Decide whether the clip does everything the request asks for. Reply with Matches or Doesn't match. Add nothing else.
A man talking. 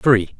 Matches